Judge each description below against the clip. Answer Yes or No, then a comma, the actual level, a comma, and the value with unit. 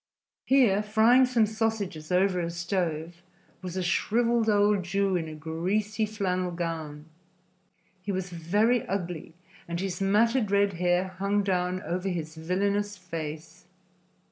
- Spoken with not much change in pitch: No, average, 3.2 semitones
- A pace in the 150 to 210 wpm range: No, slow, 135 wpm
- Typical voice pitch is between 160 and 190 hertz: Yes, medium, 185 Hz